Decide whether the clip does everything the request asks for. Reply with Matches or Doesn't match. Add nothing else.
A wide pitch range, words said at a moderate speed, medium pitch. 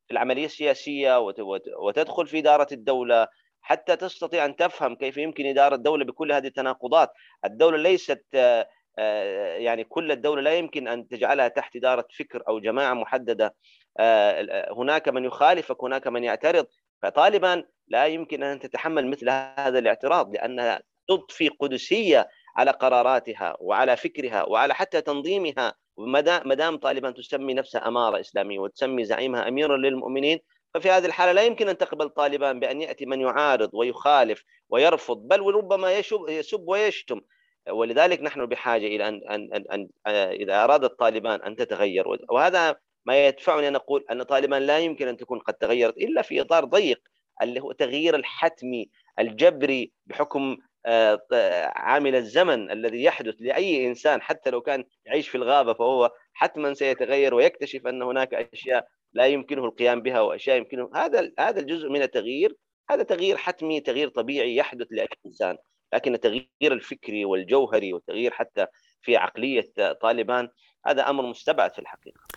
Doesn't match